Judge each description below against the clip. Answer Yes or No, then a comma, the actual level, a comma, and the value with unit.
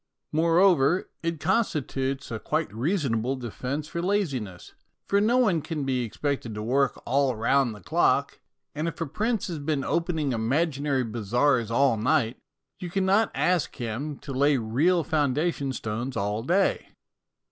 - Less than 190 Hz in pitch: Yes, medium, 140 Hz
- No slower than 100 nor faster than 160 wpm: Yes, average, 150 wpm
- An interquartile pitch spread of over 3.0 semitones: Yes, wide, 5.5 semitones